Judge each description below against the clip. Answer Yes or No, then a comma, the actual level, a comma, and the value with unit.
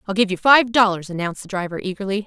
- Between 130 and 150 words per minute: No, fast, 240 wpm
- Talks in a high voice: Yes, high, 200 Hz